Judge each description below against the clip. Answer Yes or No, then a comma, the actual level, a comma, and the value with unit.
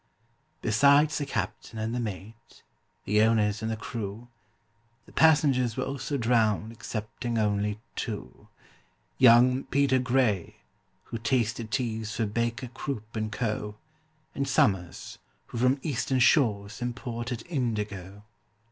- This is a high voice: No, low, 115 Hz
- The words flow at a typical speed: No, slow, 120 wpm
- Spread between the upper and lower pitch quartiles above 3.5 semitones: No, average, 3.1 semitones